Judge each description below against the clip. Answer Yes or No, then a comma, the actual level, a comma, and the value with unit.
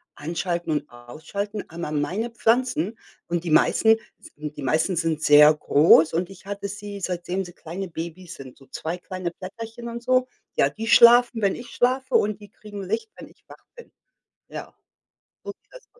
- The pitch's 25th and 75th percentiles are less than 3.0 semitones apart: No, wide, 5.5 semitones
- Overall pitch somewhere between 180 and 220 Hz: Yes, medium, 185 Hz